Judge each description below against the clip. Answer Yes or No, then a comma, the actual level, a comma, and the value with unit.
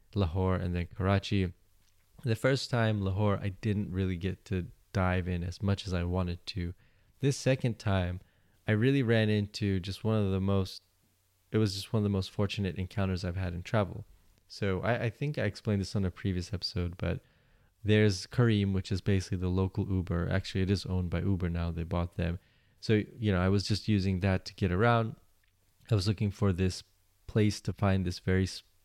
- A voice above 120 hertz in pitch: No, very low, 95 Hz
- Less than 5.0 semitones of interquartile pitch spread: Yes, narrow, 2.4 semitones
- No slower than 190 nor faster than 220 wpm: Yes, average, 200 wpm